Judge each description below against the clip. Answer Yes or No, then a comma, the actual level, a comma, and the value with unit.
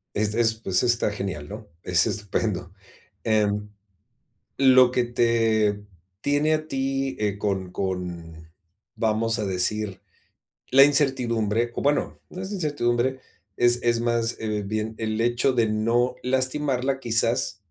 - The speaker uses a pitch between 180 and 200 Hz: No, low, 115 Hz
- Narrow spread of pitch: No, average, 3.6 semitones